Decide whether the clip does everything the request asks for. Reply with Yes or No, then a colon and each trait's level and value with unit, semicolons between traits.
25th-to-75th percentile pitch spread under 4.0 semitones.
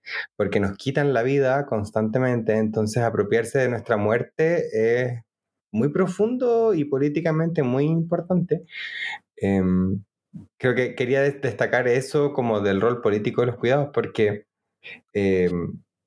No: average, 5.0 semitones